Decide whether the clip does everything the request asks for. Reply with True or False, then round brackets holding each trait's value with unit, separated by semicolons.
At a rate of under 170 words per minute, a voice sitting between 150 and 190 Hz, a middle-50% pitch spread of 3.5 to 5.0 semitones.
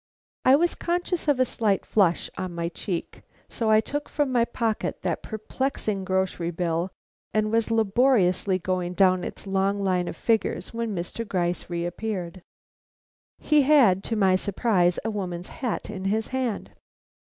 False (155 wpm; 200 Hz; 4.2 semitones)